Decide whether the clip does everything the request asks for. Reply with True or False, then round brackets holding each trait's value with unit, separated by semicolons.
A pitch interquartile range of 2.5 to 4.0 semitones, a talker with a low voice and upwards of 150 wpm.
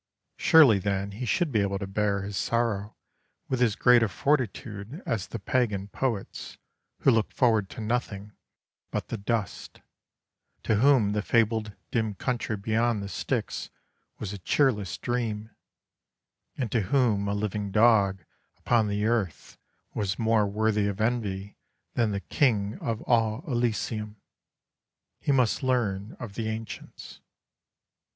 False (2.8 semitones; 110 Hz; 140 wpm)